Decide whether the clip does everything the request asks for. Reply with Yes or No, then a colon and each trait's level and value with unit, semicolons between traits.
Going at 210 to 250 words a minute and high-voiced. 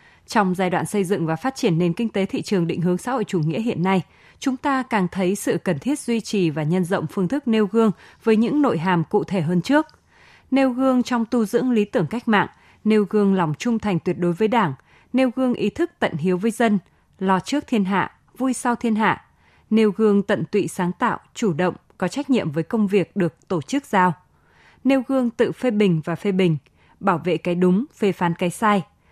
Yes: average, 235 wpm; high, 205 Hz